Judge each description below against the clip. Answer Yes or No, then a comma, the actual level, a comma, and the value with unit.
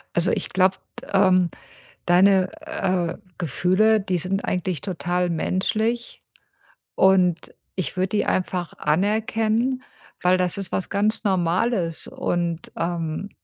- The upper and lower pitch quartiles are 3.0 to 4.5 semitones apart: No, narrow, 2.4 semitones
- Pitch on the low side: No, medium, 185 Hz